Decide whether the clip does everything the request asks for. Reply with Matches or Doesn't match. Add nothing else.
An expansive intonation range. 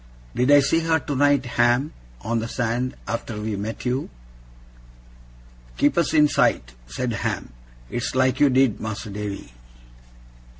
Doesn't match